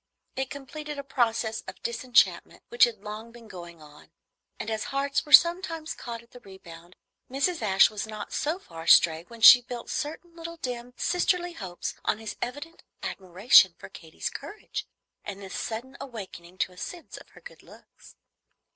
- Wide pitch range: Yes, wide, 7.2 semitones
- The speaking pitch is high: Yes, high, 235 Hz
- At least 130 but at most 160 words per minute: No, average, 175 wpm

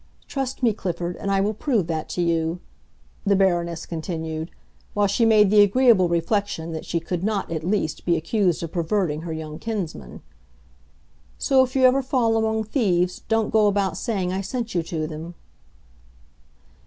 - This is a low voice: No, high, 190 Hz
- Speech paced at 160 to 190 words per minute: Yes, average, 170 wpm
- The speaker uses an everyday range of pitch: Yes, average, 4.8 semitones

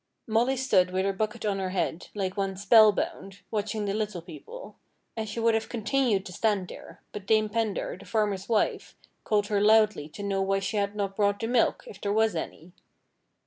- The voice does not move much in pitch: Yes, narrow, 2.2 semitones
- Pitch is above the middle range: Yes, high, 205 Hz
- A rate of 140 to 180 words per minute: No, fast, 205 wpm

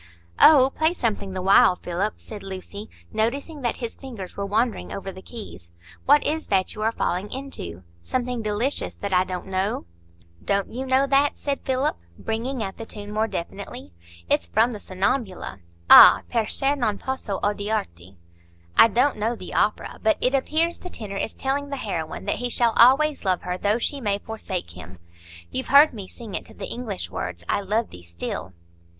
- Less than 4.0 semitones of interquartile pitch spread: No, wide, 5.4 semitones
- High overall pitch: Yes, high, 215 Hz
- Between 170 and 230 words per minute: Yes, average, 180 wpm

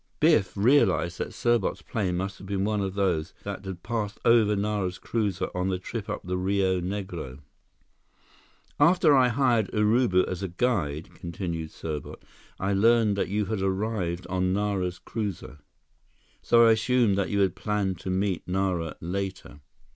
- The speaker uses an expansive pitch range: No, average, 2.9 semitones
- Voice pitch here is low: Yes, low, 100 Hz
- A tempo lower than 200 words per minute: Yes, average, 155 wpm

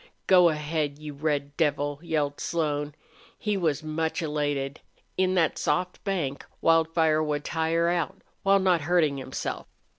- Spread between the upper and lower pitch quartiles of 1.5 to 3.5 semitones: Yes, average, 2.7 semitones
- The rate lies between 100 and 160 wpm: Yes, average, 140 wpm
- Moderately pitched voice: Yes, medium, 155 Hz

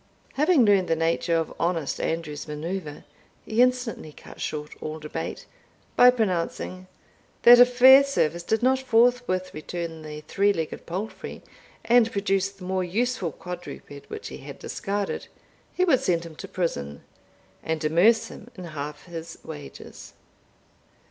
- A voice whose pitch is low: No, medium, 180 Hz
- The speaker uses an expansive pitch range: Yes, wide, 6.1 semitones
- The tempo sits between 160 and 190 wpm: No, average, 140 wpm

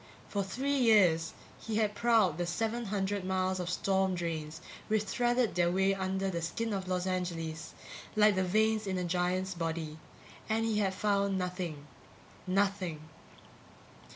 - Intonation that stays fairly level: No, average, 3.0 semitones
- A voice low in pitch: No, high, 190 Hz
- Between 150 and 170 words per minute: Yes, average, 155 wpm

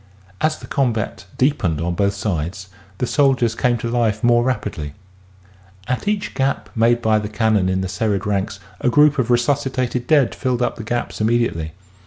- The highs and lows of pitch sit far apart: No, average, 4.0 semitones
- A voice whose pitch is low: Yes, low, 115 Hz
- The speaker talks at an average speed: Yes, average, 180 wpm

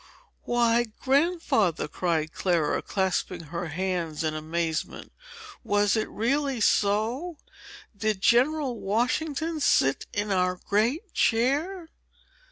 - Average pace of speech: No, slow, 100 wpm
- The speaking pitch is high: Yes, high, 215 Hz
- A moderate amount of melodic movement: No, wide, 7.2 semitones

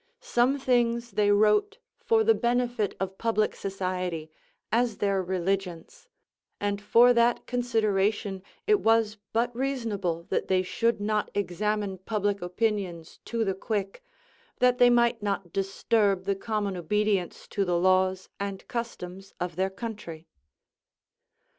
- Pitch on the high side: Yes, high, 205 Hz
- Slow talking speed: Yes, slow, 130 wpm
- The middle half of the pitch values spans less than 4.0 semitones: Yes, average, 3.5 semitones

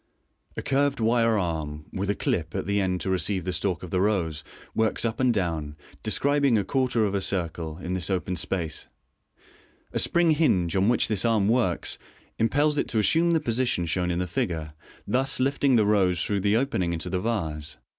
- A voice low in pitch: Yes, low, 100 Hz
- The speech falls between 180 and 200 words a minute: Yes, average, 195 wpm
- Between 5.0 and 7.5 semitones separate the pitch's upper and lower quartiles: Yes, average, 5.3 semitones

